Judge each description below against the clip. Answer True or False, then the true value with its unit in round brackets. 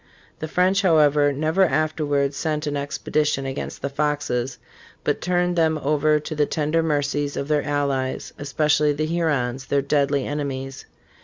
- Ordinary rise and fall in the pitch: False (1.8 semitones)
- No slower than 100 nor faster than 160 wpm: True (155 wpm)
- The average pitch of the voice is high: False (150 Hz)